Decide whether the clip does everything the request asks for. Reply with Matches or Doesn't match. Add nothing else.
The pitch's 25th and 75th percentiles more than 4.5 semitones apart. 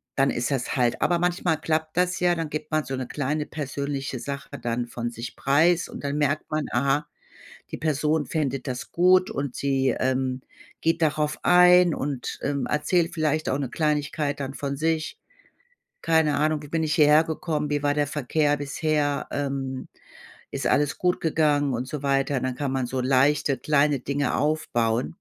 Doesn't match